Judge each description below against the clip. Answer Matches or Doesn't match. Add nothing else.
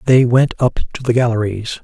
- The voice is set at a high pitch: Doesn't match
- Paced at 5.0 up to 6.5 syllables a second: Matches